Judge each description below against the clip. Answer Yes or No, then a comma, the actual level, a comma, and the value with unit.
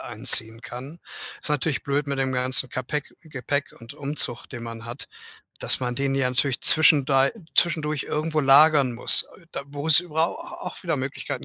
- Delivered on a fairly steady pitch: No, average, 3.0 semitones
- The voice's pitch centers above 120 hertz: Yes, medium, 140 Hz